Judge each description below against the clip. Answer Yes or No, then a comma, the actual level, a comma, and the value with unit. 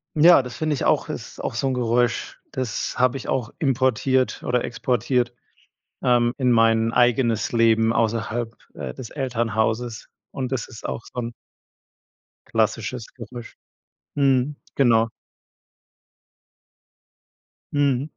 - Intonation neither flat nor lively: No, narrow, 2.3 semitones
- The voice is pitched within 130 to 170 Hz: No, low, 120 Hz